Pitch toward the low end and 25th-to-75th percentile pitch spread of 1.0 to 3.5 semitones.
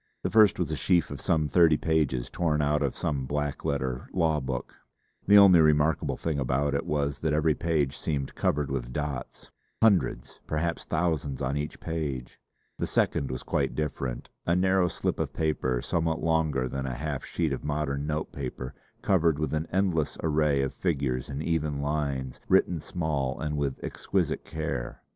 Yes: very low, 75 Hz; average, 2.9 semitones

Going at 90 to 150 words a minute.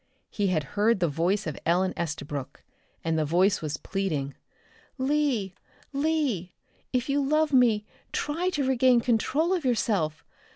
Yes: average, 140 wpm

